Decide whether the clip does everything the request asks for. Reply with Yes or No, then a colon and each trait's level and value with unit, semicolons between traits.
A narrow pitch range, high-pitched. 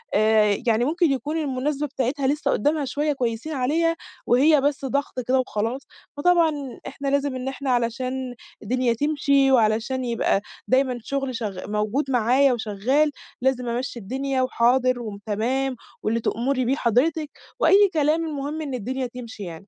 No: average, 3.2 semitones; very high, 260 Hz